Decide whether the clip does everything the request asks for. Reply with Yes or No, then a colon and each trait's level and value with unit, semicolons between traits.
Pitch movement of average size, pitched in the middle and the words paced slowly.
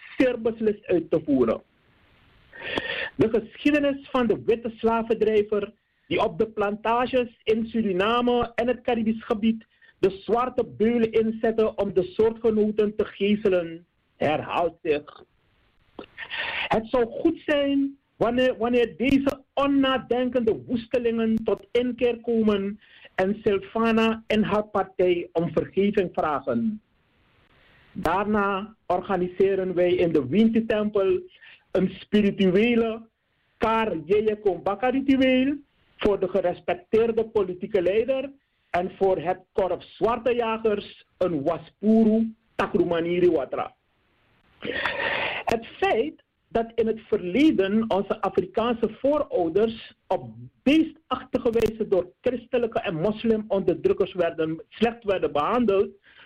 No: average, 3.7 semitones; high, 220 Hz; slow, 100 wpm